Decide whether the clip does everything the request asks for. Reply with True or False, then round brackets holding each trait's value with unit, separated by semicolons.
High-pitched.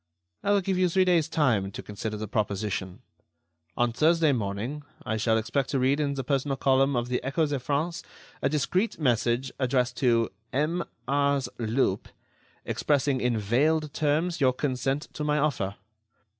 False (135 Hz)